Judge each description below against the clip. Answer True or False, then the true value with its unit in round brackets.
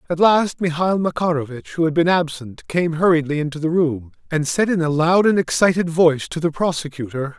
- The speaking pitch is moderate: True (160 Hz)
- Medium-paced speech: True (195 wpm)